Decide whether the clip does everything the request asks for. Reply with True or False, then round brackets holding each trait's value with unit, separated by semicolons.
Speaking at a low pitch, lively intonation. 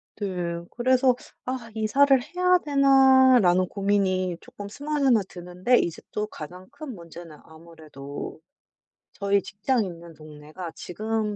False (200 Hz; 6.8 semitones)